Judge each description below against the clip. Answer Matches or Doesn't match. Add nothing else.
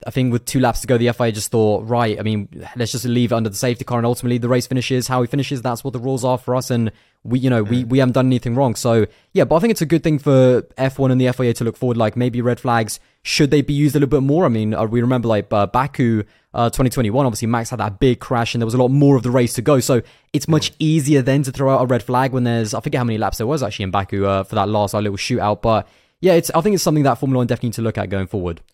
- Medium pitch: Doesn't match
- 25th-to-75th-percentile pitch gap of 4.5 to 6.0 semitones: Doesn't match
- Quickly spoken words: Matches